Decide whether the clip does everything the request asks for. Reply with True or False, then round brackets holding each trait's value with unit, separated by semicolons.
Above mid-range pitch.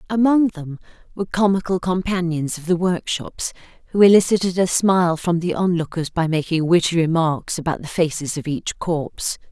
False (175 Hz)